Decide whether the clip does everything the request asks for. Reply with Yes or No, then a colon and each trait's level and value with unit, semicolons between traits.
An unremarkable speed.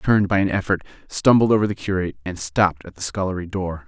No: fast, 230 wpm